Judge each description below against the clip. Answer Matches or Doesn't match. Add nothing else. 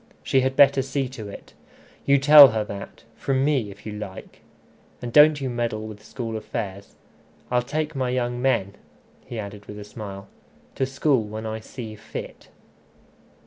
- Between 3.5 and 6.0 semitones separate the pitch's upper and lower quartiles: Matches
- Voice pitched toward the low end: Matches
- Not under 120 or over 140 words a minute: Doesn't match